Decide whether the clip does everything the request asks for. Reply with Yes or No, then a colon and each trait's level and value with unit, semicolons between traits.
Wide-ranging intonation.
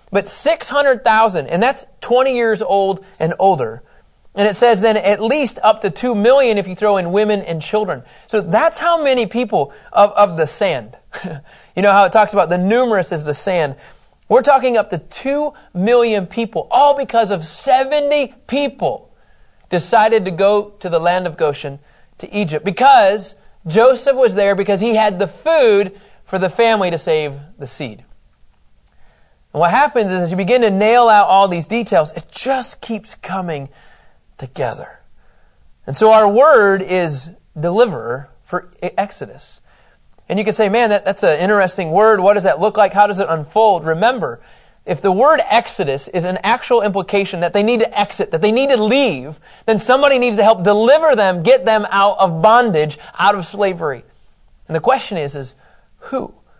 No: average, 4.1 semitones